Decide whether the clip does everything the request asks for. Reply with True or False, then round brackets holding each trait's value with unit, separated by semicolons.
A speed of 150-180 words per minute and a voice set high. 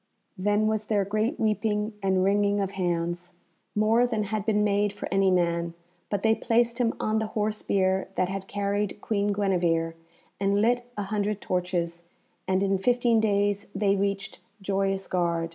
True (165 wpm; 200 Hz)